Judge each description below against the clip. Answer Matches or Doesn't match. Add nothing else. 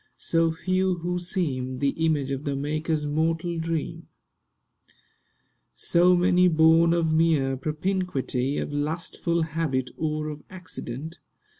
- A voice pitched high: Doesn't match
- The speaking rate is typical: Doesn't match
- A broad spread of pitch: Doesn't match